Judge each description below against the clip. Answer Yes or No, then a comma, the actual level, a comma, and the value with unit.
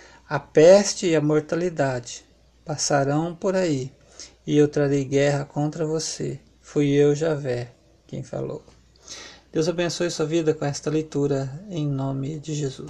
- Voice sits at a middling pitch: Yes, medium, 150 Hz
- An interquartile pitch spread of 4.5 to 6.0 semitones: No, narrow, 2.6 semitones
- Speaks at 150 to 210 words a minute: No, average, 140 wpm